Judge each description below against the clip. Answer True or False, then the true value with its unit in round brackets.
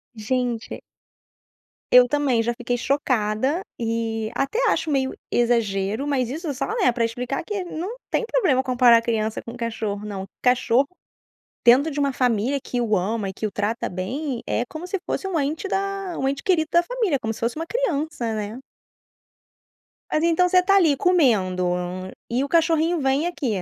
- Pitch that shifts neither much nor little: False (5.9 semitones)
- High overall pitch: True (260 Hz)